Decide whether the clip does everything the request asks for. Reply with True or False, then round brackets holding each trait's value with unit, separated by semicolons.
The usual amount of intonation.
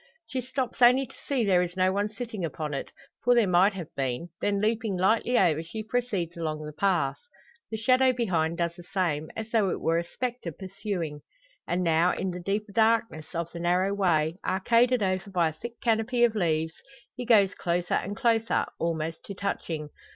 True (4.9 semitones)